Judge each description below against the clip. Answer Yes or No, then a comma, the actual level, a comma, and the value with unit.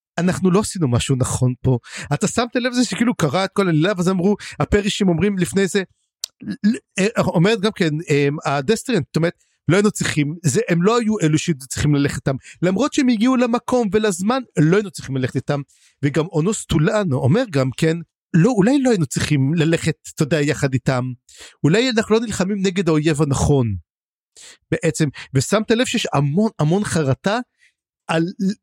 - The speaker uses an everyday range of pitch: No, wide, 6.1 semitones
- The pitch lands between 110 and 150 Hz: No, medium, 170 Hz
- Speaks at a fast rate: Yes, fast, 170 wpm